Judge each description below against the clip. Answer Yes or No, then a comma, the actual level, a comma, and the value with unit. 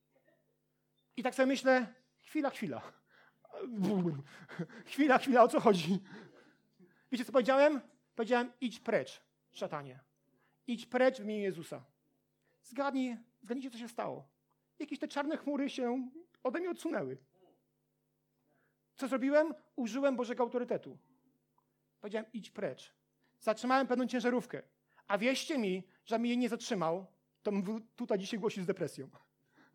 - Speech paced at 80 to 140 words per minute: Yes, average, 125 wpm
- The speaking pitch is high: Yes, high, 240 Hz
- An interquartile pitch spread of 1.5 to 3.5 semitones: No, average, 4.7 semitones